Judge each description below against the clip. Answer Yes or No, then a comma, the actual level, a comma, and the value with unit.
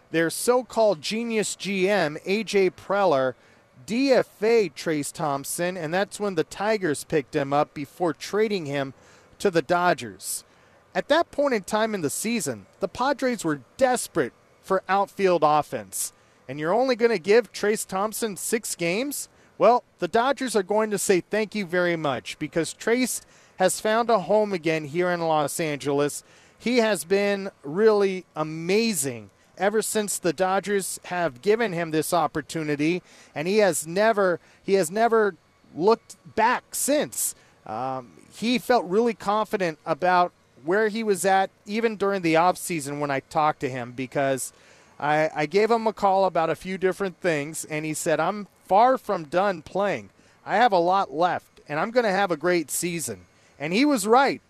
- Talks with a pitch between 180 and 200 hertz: Yes, medium, 185 Hz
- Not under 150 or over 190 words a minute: Yes, average, 165 wpm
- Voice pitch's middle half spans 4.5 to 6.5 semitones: Yes, wide, 5.6 semitones